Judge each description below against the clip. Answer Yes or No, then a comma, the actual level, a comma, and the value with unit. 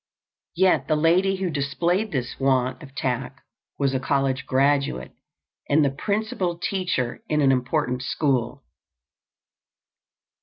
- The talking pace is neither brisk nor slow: No, slow, 120 wpm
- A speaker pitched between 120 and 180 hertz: Yes, medium, 140 Hz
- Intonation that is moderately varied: Yes, average, 4.6 semitones